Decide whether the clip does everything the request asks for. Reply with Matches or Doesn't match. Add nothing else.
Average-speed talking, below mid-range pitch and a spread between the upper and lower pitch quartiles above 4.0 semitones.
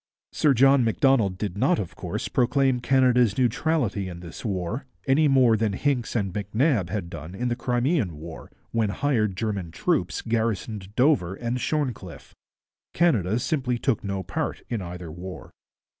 Matches